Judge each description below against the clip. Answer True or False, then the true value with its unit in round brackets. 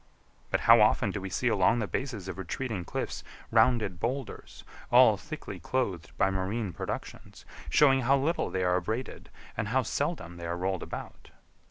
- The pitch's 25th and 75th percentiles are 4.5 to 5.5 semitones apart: True (5.1 semitones)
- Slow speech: False (170 wpm)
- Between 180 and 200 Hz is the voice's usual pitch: False (105 Hz)